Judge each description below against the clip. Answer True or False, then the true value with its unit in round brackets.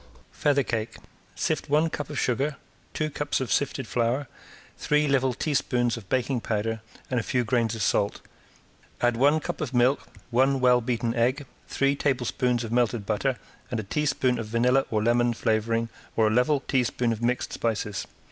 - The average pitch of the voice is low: True (125 Hz)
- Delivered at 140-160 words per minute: False (175 wpm)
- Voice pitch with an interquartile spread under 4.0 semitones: True (2.9 semitones)